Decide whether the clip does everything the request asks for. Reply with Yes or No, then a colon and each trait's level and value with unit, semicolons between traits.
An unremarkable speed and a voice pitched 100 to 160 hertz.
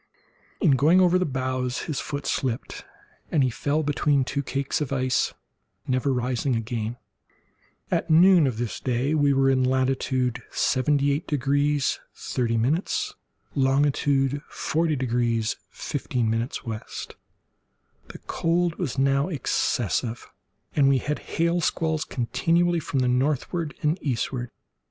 No: slow, 125 wpm; low, 135 Hz